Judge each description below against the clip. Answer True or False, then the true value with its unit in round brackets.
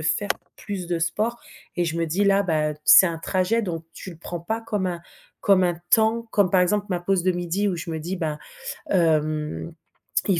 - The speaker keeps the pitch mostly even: False (3.2 semitones)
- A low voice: False (175 Hz)